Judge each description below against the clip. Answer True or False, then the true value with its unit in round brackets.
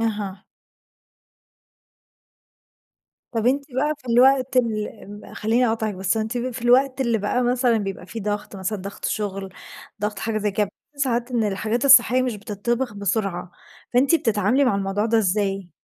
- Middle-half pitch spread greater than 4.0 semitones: False (3.6 semitones)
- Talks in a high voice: True (220 Hz)